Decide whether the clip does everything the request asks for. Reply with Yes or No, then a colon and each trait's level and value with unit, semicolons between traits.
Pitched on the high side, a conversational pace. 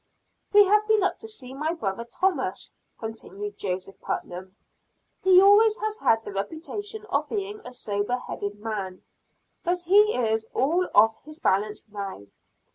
Yes: very high, 255 Hz; average, 150 wpm